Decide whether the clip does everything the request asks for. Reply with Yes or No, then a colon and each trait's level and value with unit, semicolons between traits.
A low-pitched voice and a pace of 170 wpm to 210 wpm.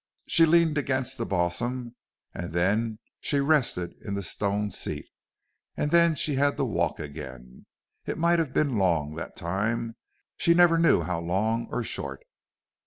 No: low, 115 Hz; average, 160 wpm